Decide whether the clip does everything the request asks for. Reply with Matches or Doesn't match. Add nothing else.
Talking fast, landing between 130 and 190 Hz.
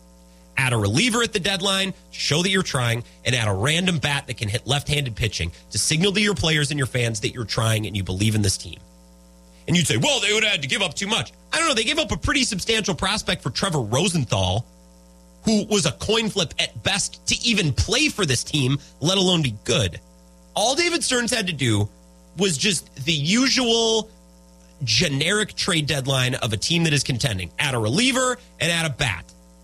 Matches